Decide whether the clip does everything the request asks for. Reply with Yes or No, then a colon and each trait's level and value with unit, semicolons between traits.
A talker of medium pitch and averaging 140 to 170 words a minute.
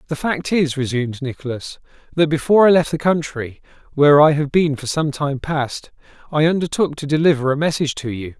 No: medium, 145 Hz; average, 195 wpm